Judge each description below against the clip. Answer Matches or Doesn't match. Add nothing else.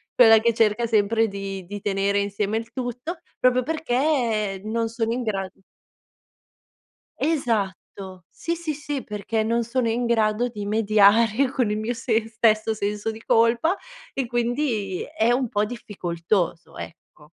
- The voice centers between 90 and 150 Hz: Doesn't match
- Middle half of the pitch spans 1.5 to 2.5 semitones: Doesn't match